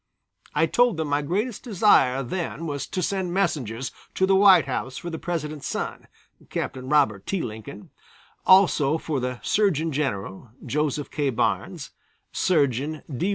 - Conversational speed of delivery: Yes, average, 150 wpm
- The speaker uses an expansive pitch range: Yes, wide, 5.7 semitones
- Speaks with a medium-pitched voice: Yes, medium, 150 Hz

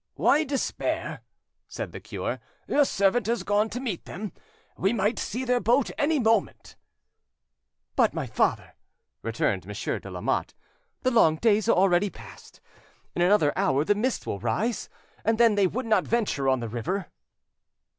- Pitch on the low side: No, high, 210 Hz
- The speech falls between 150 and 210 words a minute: Yes, average, 160 wpm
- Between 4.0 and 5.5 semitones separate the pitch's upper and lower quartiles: Yes, average, 4.7 semitones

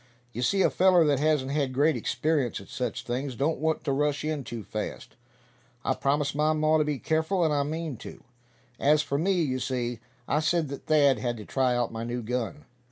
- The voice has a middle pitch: Yes, medium, 145 Hz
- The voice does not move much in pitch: No, average, 3.7 semitones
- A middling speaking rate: No, fast, 215 wpm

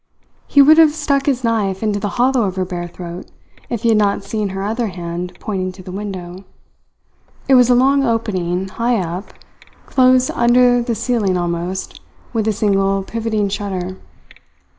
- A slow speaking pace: No, average, 170 wpm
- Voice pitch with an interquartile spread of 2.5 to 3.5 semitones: No, average, 4.4 semitones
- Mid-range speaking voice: No, high, 205 Hz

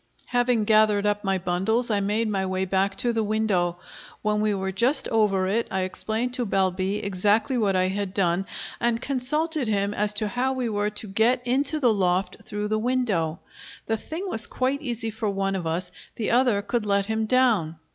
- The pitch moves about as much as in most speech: Yes, average, 3.6 semitones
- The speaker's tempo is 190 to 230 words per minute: Yes, average, 195 wpm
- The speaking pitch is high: Yes, high, 210 Hz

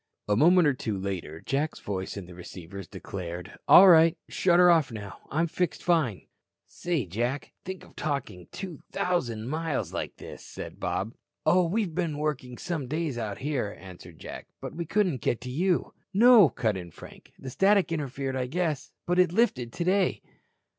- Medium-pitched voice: Yes, medium, 145 Hz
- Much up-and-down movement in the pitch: Yes, wide, 8.2 semitones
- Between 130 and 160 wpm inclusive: No, average, 170 wpm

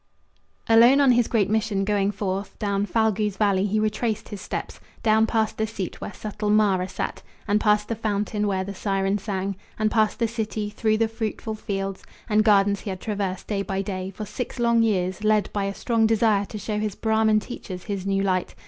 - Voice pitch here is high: Yes, high, 210 Hz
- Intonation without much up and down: Yes, narrow, 1.8 semitones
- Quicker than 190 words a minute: Yes, average, 200 wpm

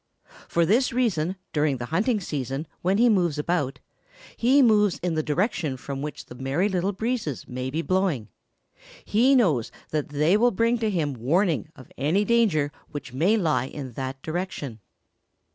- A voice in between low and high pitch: Yes, medium, 165 Hz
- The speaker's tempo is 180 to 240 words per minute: No, average, 165 wpm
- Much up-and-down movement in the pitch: Yes, wide, 6.8 semitones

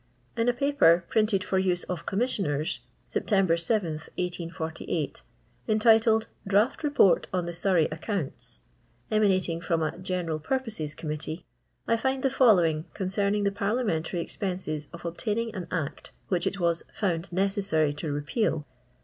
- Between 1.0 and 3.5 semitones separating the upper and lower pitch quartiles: No, average, 4.6 semitones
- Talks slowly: No, average, 150 wpm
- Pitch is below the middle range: No, medium, 185 Hz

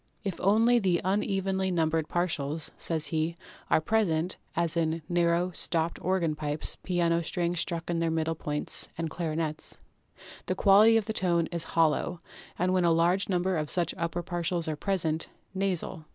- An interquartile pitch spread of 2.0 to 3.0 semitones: Yes, narrow, 2.4 semitones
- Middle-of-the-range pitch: Yes, medium, 170 Hz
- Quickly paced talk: No, average, 165 wpm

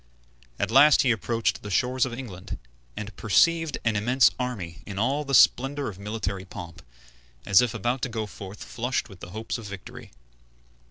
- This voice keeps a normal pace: Yes, average, 170 wpm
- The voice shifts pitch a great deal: No, average, 4.2 semitones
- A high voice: No, low, 115 Hz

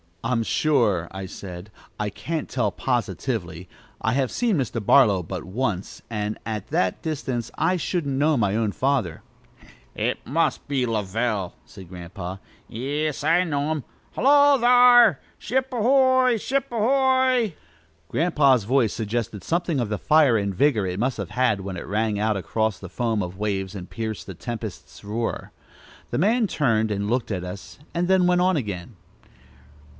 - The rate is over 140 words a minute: Yes, average, 160 wpm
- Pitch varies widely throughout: Yes, wide, 8.2 semitones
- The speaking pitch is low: Yes, low, 120 Hz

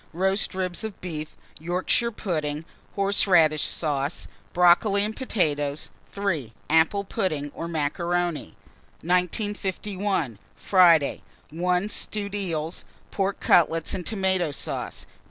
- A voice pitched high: No, medium, 180 Hz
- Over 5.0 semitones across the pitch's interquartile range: No, average, 4.0 semitones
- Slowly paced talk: Yes, slow, 100 wpm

